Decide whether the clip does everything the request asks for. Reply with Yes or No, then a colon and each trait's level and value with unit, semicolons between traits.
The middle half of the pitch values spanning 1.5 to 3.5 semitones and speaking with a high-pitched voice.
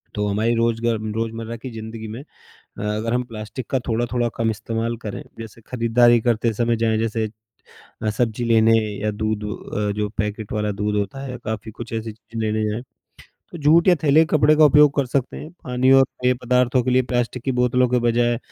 No: narrow, 2.4 semitones; low, 115 Hz